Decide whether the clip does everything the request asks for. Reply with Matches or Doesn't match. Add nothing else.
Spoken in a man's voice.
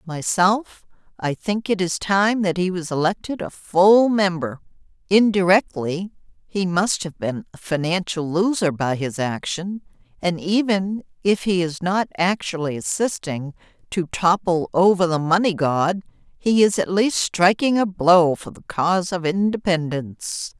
Doesn't match